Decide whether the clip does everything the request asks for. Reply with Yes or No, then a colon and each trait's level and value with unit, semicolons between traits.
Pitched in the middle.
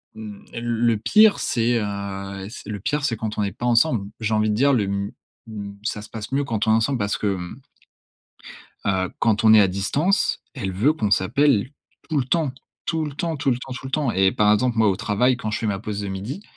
No: low, 110 Hz